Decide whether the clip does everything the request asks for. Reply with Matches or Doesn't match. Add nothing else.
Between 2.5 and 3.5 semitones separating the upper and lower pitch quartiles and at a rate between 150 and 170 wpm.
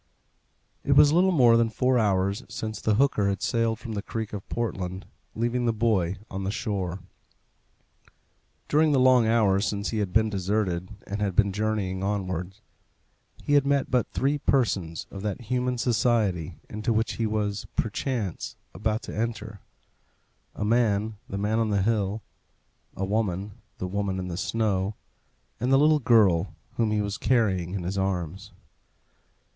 Matches